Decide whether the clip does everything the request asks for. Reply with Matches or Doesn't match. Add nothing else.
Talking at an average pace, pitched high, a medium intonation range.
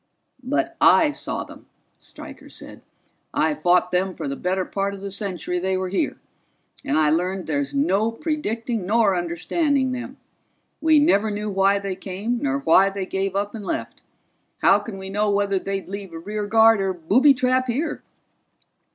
Matches